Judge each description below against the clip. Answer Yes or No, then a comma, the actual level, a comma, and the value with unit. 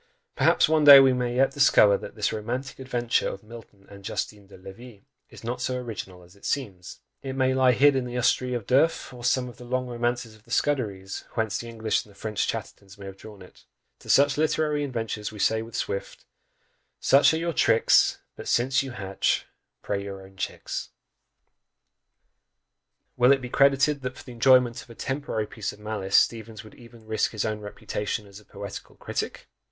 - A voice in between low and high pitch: No, low, 115 Hz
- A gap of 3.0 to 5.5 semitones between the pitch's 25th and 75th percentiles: Yes, average, 3.9 semitones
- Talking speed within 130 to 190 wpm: No, average, 200 wpm